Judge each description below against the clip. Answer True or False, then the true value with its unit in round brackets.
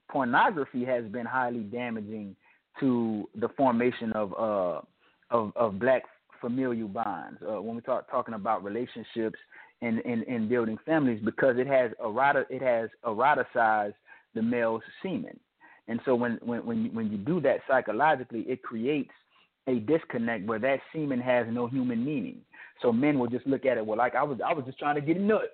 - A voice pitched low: True (125 Hz)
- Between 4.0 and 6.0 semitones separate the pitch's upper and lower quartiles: True (4.4 semitones)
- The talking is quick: False (180 wpm)